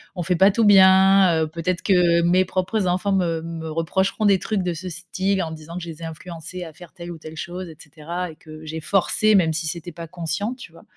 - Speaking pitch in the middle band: Yes, medium, 175 Hz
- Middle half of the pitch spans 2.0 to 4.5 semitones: Yes, narrow, 2.5 semitones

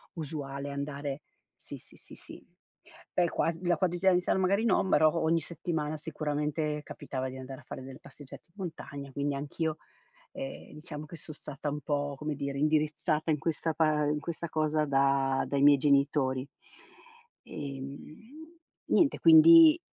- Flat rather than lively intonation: No, average, 3.0 semitones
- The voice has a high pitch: No, medium, 150 Hz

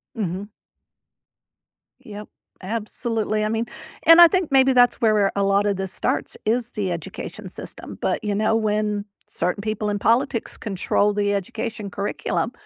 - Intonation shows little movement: Yes, narrow, 2.1 semitones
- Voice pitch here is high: Yes, high, 210 Hz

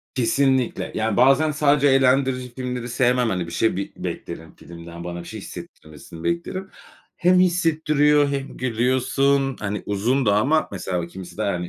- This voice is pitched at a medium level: No, low, 125 Hz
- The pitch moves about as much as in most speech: No, wide, 5.9 semitones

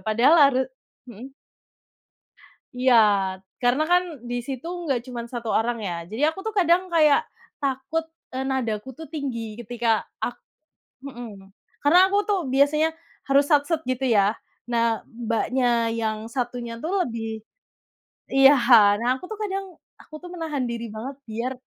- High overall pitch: Yes, very high, 255 Hz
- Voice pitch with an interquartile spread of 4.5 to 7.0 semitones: Yes, average, 4.9 semitones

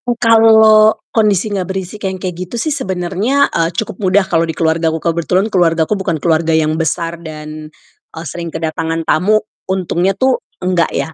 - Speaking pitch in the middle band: Yes, medium, 180 Hz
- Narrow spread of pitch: No, average, 4.2 semitones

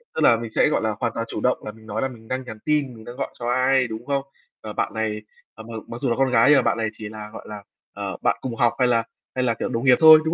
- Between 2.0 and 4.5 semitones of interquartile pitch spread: Yes, average, 2.8 semitones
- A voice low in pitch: Yes, low, 120 Hz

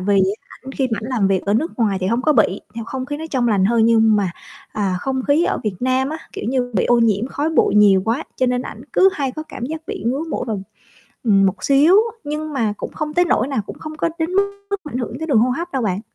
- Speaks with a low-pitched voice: No, very high, 250 Hz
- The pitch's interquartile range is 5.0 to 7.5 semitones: Yes, wide, 5.4 semitones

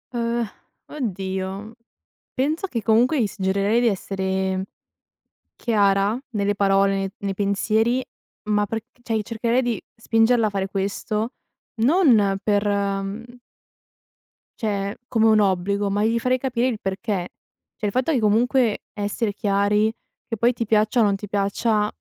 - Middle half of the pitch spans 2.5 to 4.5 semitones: Yes, average, 2.8 semitones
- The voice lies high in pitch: Yes, high, 210 Hz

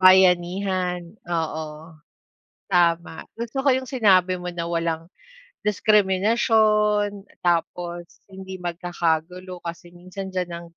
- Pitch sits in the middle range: Yes, medium, 180 Hz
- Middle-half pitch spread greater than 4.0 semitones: No, average, 2.7 semitones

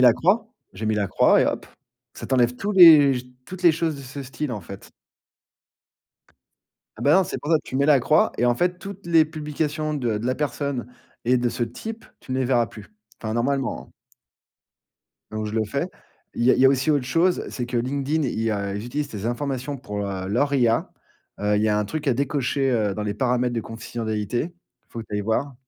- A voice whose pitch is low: Yes, low, 130 Hz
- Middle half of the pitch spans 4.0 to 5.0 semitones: Yes, average, 4.7 semitones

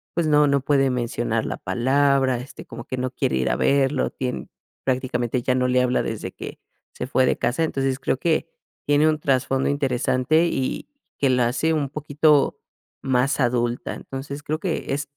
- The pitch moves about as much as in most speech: No, narrow, 2.3 semitones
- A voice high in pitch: No, low, 135 Hz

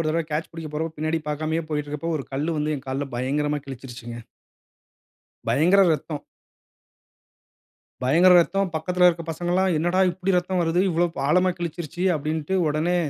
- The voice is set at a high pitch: No, medium, 160 Hz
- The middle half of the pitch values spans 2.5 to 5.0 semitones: Yes, average, 3.0 semitones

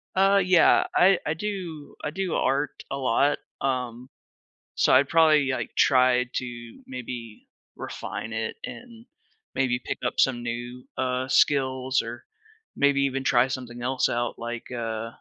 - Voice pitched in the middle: No, low, 130 Hz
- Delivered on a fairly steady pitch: No, average, 3.1 semitones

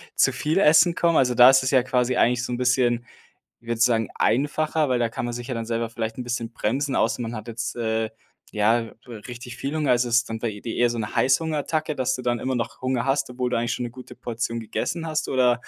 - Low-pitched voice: Yes, low, 125 Hz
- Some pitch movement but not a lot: No, narrow, 2.1 semitones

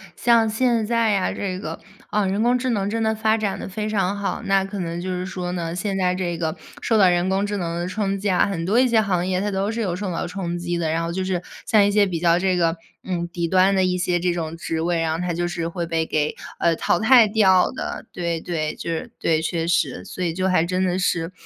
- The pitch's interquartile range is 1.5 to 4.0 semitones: Yes, average, 2.9 semitones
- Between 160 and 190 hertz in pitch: Yes, medium, 185 Hz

